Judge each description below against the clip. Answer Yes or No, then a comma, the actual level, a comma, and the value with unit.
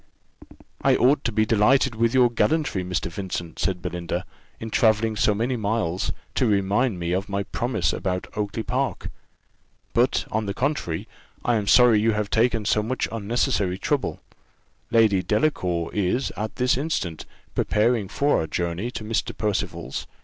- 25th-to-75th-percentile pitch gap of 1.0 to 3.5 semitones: No, average, 4.1 semitones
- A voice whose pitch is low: Yes, low, 110 Hz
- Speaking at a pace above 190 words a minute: No, average, 155 wpm